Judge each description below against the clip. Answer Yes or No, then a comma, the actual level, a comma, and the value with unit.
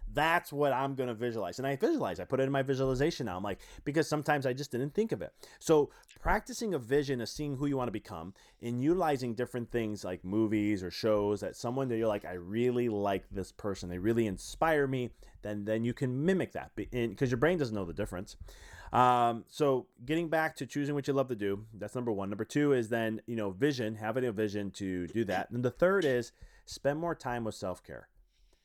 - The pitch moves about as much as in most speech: Yes, average, 5.0 semitones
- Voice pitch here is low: Yes, low, 120 Hz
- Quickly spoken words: Yes, fast, 225 wpm